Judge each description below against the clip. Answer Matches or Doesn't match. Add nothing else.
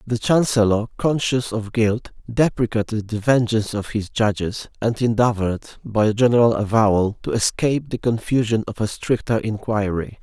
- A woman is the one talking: Doesn't match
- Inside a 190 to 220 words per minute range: Doesn't match